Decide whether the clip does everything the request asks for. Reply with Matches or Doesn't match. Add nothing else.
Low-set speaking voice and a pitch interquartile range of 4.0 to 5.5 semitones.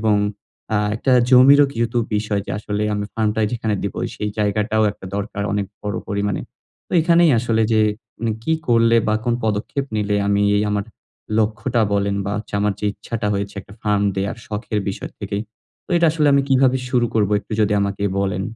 Doesn't match